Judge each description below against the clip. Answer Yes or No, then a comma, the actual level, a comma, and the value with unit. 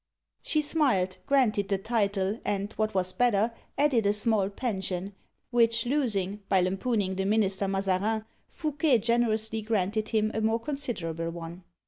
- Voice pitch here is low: No, high, 215 Hz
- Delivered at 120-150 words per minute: Yes, average, 140 wpm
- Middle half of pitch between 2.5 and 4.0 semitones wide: Yes, average, 3.4 semitones